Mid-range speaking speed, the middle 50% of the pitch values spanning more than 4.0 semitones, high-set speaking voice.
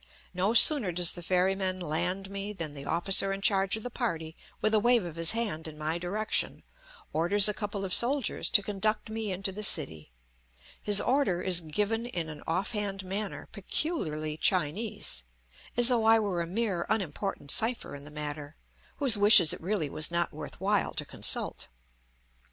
Yes: average, 180 wpm; average, 4.4 semitones; high, 195 Hz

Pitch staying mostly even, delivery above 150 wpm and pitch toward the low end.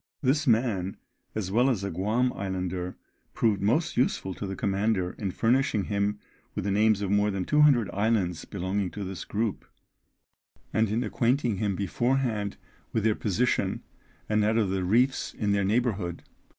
No: average, 3.2 semitones; average, 165 wpm; low, 105 Hz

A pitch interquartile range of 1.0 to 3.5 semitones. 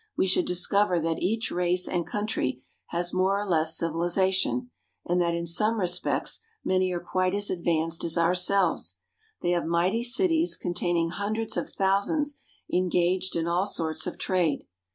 Yes: average, 2.8 semitones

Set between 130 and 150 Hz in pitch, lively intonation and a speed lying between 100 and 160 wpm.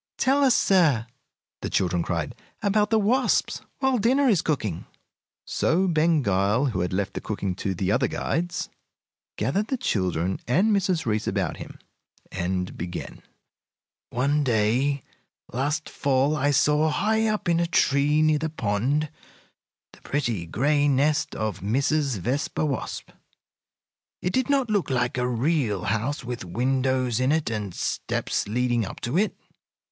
Yes: medium, 140 Hz; wide, 7.2 semitones; average, 150 wpm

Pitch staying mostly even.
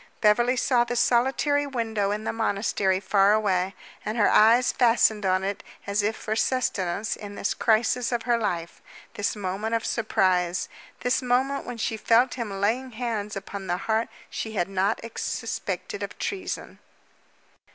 No: average, 3.3 semitones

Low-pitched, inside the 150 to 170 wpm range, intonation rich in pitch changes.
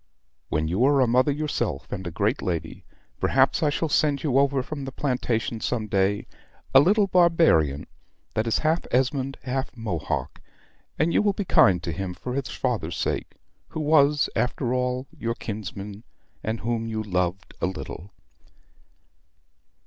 Yes: low, 125 Hz; average, 160 wpm; wide, 6.1 semitones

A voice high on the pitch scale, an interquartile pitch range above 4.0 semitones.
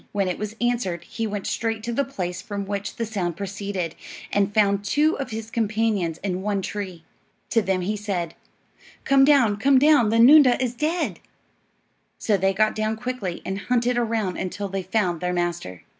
No: high, 210 Hz; average, 3.7 semitones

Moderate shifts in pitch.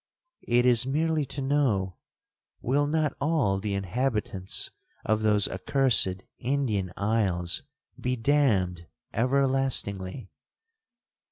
No: wide, 5.8 semitones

